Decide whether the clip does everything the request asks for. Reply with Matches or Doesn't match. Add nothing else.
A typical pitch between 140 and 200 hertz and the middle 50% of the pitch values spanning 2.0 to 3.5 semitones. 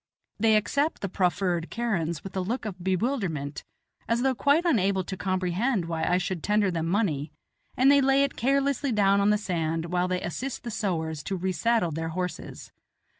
Doesn't match